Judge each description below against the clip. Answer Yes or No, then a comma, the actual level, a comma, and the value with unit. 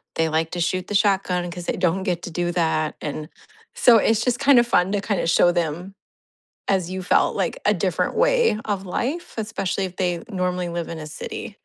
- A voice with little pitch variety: No, average, 3.3 semitones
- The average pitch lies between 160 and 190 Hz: Yes, medium, 185 Hz